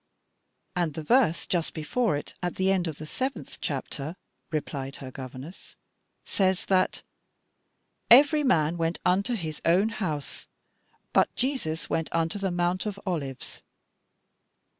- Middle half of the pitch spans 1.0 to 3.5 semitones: No, average, 4.1 semitones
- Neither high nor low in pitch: Yes, medium, 175 Hz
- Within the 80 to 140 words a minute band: Yes, slow, 135 wpm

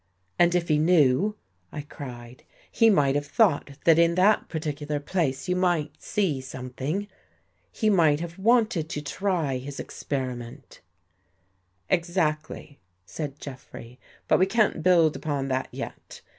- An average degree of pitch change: Yes, average, 4.8 semitones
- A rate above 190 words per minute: No, average, 155 wpm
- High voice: No, medium, 150 Hz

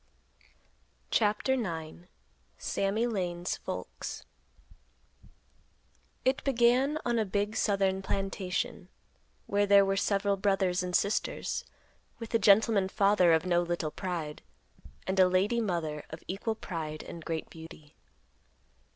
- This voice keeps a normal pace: No, slow, 115 wpm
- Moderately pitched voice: No, high, 195 Hz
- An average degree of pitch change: Yes, average, 3.3 semitones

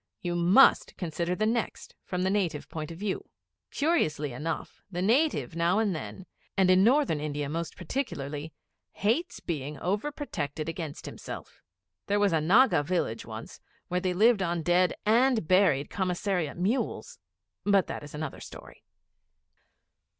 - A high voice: No, medium, 180 Hz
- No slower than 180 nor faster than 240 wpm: No, average, 150 wpm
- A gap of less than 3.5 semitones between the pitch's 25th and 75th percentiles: No, average, 4.9 semitones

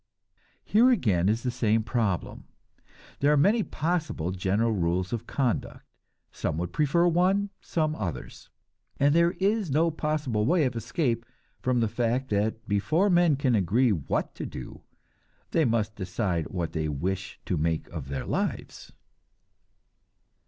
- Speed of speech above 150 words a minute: No, average, 145 wpm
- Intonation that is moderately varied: No, wide, 8.3 semitones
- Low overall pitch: Yes, low, 115 Hz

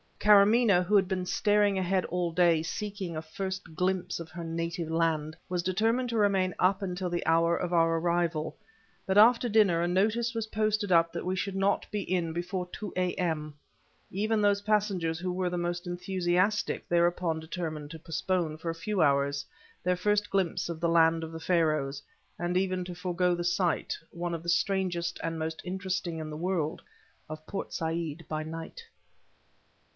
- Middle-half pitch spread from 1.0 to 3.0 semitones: Yes, average, 2.7 semitones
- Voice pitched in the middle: Yes, medium, 175 Hz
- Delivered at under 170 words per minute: No, average, 180 wpm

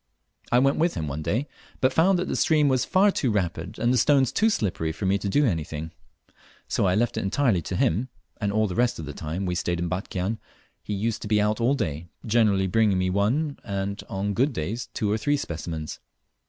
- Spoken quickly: Yes, fast, 225 wpm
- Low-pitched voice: Yes, low, 105 Hz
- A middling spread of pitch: No, wide, 5.7 semitones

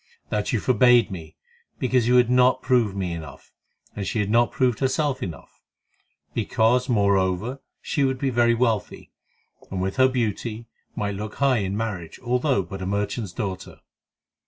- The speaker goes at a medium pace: Yes, average, 160 wpm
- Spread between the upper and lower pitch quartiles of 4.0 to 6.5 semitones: Yes, average, 4.3 semitones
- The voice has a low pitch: Yes, low, 115 Hz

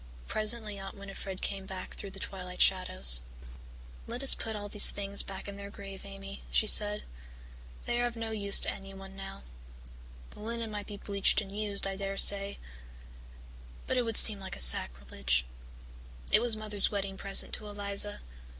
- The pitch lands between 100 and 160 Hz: No, high, 200 Hz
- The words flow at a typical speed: Yes, average, 175 wpm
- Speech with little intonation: Yes, narrow, 1.5 semitones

